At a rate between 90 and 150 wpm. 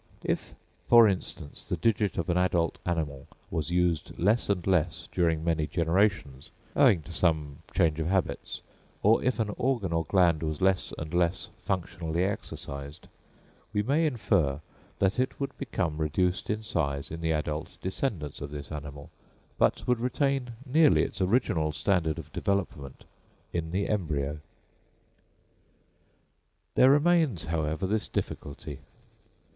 Yes: average, 140 wpm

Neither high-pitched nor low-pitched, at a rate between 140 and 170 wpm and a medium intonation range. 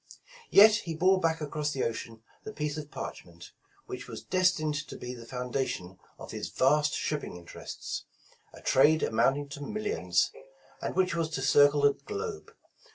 Yes: medium, 150 Hz; average, 165 wpm; average, 4.4 semitones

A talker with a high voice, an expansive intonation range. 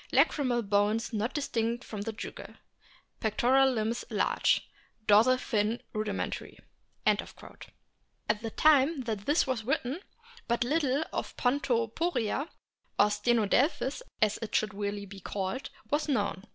No: high, 230 Hz; average, 4.1 semitones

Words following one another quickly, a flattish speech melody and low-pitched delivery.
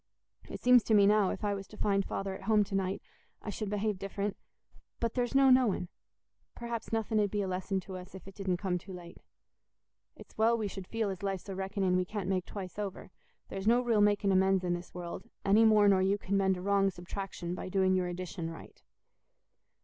No: fast, 220 wpm; narrow, 2.1 semitones; high, 195 Hz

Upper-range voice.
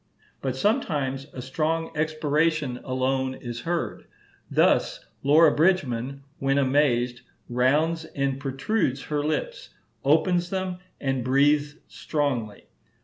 No: medium, 140 Hz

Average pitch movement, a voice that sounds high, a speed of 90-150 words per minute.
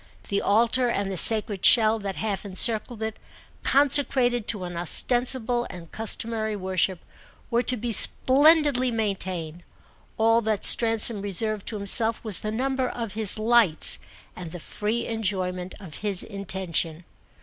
Yes: average, 3.6 semitones; high, 215 Hz; average, 140 wpm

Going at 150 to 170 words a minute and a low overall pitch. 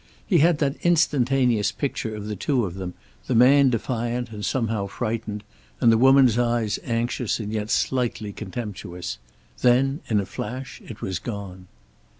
Yes: average, 155 wpm; low, 115 Hz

